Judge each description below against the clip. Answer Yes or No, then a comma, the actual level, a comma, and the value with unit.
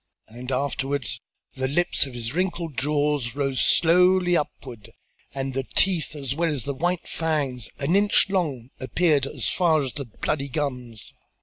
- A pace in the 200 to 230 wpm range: No, average, 155 wpm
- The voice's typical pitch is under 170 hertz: Yes, medium, 140 Hz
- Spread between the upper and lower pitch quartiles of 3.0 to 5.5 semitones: Yes, average, 4.2 semitones